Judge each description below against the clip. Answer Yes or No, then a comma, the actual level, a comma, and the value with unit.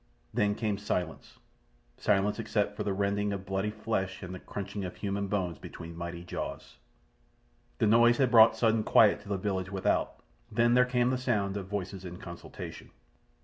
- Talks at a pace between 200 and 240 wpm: No, average, 170 wpm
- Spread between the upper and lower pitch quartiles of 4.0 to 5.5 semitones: No, narrow, 2.4 semitones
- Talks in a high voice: No, low, 100 Hz